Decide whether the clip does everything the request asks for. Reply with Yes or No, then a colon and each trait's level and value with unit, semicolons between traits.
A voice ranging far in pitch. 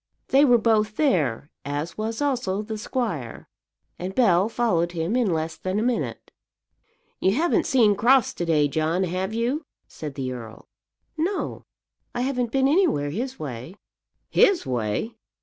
Yes: wide, 7.6 semitones